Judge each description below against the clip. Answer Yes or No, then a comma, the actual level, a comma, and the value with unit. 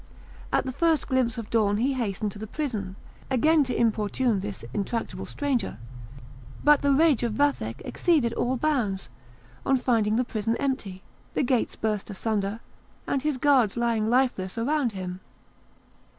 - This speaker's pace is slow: No, average, 150 wpm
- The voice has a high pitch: Yes, high, 235 Hz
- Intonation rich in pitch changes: No, average, 4.3 semitones